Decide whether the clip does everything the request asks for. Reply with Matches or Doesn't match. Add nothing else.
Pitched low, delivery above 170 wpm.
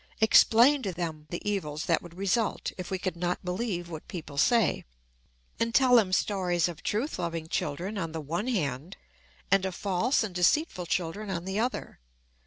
Doesn't match